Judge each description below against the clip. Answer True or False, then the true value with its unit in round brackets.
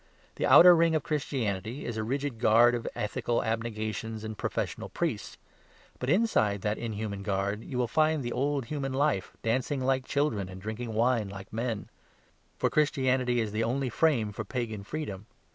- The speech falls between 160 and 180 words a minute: True (170 wpm)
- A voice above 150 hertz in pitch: False (120 Hz)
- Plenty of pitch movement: False (4.1 semitones)